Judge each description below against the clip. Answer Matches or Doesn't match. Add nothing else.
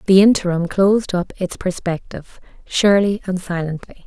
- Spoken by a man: Doesn't match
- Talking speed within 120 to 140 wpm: Matches